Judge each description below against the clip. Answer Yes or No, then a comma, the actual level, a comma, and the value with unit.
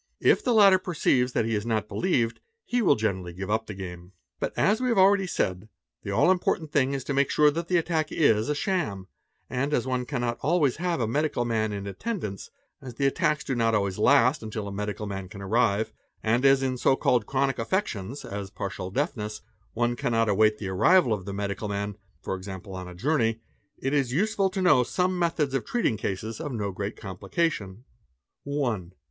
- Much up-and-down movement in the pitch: Yes, wide, 6.7 semitones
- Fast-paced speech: Yes, fast, 210 wpm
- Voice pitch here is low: Yes, low, 120 Hz